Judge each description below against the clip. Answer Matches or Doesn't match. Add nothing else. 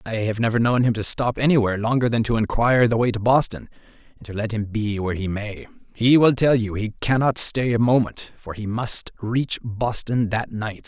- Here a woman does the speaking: Doesn't match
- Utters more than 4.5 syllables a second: Matches